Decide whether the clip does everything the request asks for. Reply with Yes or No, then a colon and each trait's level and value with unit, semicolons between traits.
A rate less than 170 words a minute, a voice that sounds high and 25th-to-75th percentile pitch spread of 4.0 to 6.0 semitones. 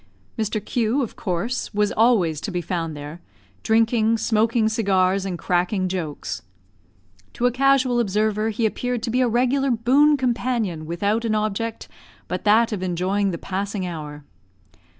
Yes: average, 150 wpm; high, 215 Hz; average, 4.4 semitones